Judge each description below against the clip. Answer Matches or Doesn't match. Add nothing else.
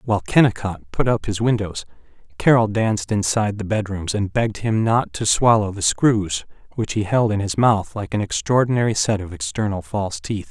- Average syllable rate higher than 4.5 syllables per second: Matches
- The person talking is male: Matches